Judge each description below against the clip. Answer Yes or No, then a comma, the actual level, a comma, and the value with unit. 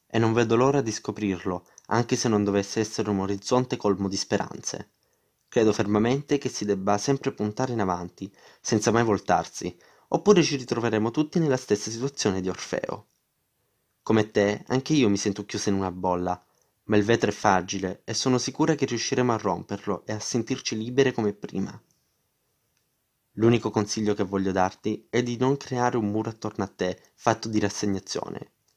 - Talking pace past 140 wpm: Yes, fast, 170 wpm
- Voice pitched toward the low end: Yes, low, 110 Hz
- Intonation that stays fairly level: No, average, 3.7 semitones